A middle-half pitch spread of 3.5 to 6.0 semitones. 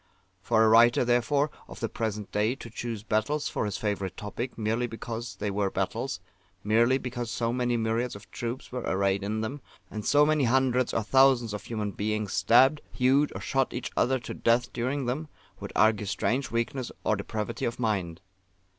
No: average, 3.0 semitones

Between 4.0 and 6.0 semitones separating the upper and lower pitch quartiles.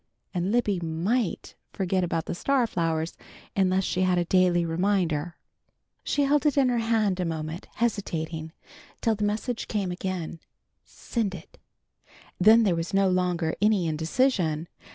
Yes: average, 4.4 semitones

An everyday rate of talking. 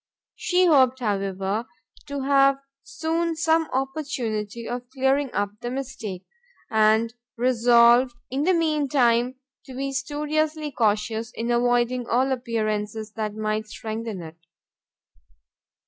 No: slow, 115 wpm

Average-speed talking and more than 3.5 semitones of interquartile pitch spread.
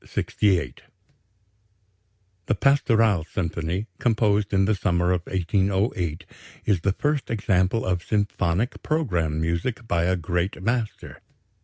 No: slow, 115 wpm; average, 4.0 semitones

